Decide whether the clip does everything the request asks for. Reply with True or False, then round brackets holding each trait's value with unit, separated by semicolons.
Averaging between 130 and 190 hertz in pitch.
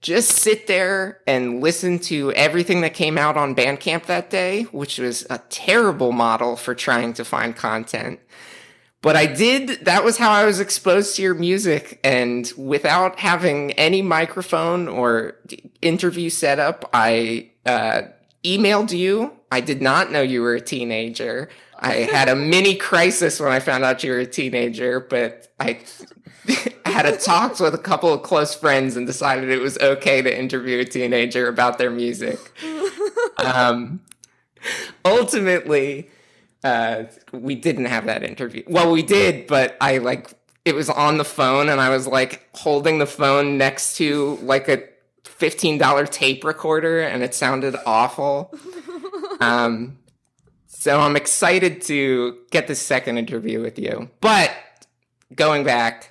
True (140 Hz)